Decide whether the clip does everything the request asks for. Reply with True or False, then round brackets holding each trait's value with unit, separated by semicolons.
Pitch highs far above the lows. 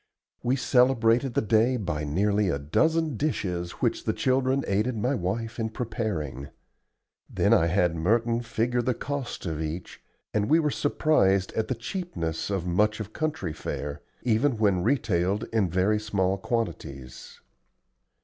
True (5.7 semitones)